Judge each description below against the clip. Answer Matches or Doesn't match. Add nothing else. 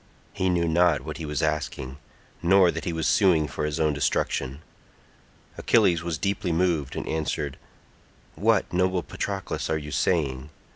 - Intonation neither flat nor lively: Matches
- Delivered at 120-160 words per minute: Matches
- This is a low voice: Matches